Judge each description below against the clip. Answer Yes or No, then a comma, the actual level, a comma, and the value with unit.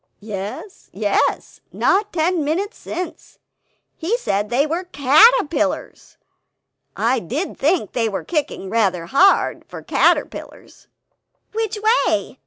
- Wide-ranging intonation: Yes, wide, 8.8 semitones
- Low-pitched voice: No, very high, 310 Hz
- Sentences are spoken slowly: Yes, slow, 110 wpm